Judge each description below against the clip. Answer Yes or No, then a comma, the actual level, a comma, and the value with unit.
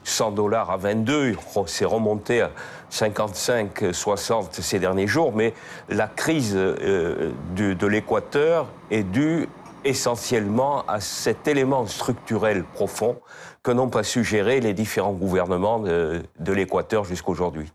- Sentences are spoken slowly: Yes, slow, 125 wpm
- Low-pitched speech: Yes, low, 110 Hz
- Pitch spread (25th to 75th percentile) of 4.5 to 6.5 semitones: Yes, average, 4.9 semitones